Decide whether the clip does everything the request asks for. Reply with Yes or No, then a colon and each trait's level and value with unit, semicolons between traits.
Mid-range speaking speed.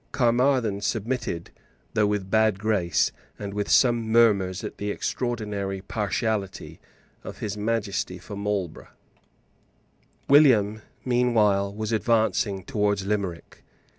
No: slow, 110 wpm